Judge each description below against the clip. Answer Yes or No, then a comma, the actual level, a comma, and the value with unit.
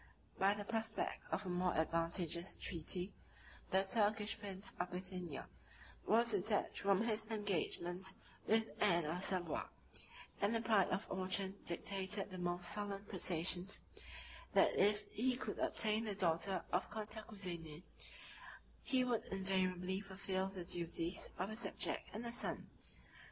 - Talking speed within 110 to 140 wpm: Yes, slow, 135 wpm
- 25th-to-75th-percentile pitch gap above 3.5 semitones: No, average, 2.8 semitones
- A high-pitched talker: Yes, high, 195 Hz